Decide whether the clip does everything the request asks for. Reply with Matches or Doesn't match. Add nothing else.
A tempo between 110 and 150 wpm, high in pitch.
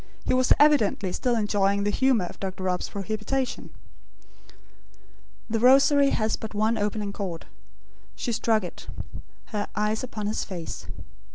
Matches